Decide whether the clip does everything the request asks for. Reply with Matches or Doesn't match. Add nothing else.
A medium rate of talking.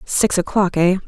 Matches